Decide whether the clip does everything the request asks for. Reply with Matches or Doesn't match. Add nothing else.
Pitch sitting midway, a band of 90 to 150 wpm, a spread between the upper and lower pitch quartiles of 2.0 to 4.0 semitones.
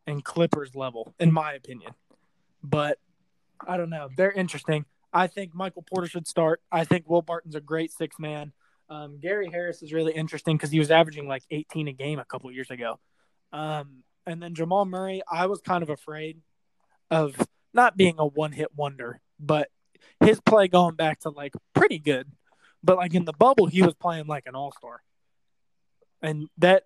Doesn't match